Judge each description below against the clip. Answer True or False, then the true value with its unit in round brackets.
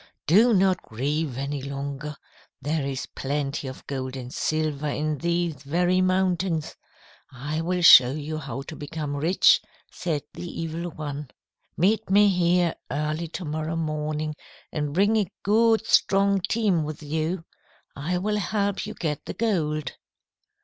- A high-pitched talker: False (155 Hz)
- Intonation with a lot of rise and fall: False (4.0 semitones)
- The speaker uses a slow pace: False (145 wpm)